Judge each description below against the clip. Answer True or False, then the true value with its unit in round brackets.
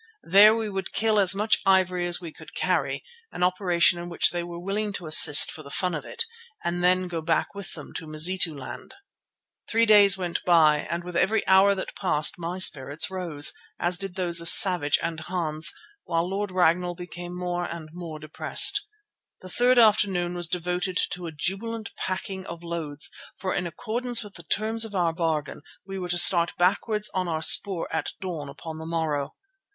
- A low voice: False (180 Hz)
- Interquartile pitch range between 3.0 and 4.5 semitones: False (2.6 semitones)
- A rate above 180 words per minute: True (190 wpm)